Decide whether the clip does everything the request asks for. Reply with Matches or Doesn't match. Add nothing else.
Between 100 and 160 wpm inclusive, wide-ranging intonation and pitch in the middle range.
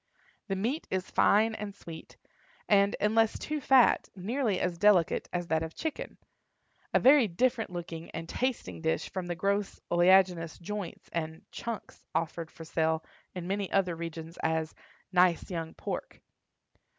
Doesn't match